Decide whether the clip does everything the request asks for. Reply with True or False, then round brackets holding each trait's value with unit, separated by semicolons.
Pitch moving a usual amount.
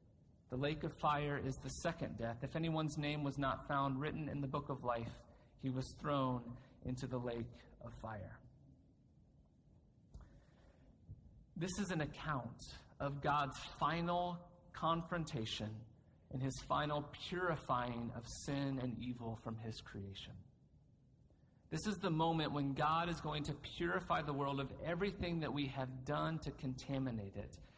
True (3.8 semitones)